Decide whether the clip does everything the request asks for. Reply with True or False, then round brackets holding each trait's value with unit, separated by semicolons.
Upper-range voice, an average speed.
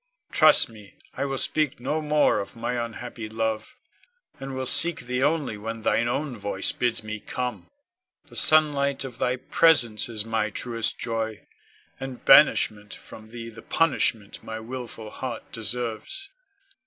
False (120 Hz; 150 wpm)